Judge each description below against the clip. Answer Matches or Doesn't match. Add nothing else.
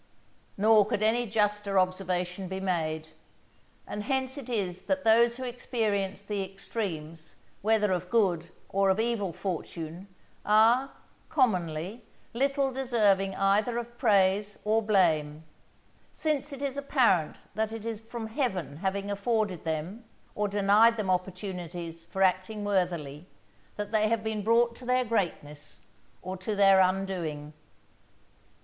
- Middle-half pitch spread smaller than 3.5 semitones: Doesn't match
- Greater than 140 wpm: Doesn't match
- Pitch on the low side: Doesn't match